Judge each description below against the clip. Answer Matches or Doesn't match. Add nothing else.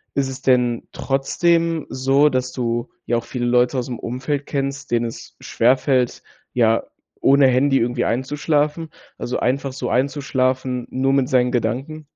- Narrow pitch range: Matches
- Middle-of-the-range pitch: Doesn't match